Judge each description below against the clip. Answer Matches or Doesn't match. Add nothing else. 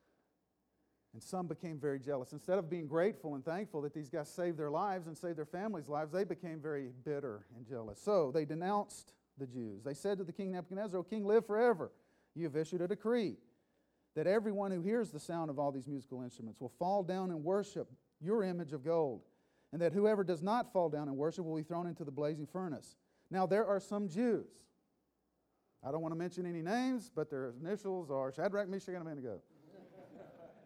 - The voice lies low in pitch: Doesn't match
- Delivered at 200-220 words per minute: Matches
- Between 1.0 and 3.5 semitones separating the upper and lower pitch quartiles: Doesn't match